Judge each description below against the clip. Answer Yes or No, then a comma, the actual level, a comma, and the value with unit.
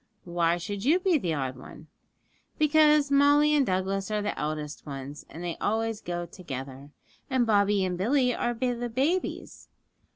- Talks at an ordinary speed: Yes, average, 160 wpm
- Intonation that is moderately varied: No, wide, 7.8 semitones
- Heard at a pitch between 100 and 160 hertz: No, high, 205 Hz